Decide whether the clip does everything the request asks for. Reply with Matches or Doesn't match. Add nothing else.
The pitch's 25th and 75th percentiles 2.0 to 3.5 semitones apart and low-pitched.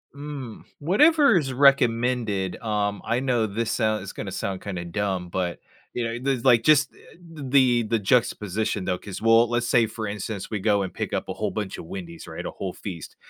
Doesn't match